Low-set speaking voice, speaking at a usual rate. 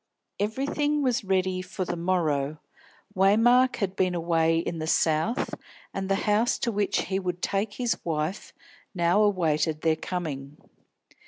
No: medium, 185 Hz; average, 145 wpm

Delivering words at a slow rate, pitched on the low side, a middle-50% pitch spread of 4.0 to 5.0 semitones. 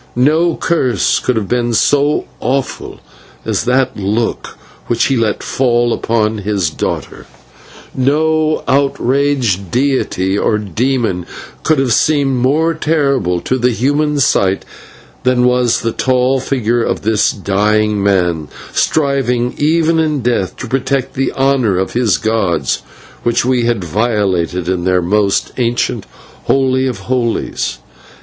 Yes: slow, 130 wpm; low, 120 Hz; average, 4.5 semitones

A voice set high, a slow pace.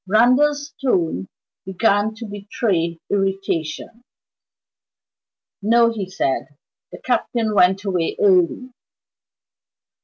Yes: high, 200 Hz; slow, 85 wpm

